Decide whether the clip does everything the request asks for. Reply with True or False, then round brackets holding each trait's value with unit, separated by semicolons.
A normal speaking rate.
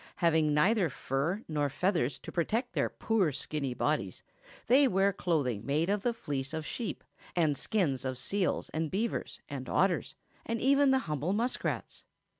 True (160 wpm)